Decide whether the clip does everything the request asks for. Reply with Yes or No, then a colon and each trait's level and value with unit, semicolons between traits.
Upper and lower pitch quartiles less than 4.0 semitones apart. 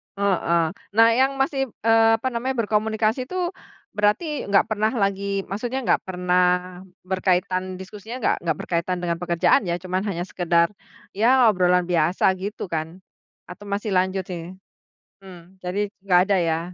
Yes: average, 3.6 semitones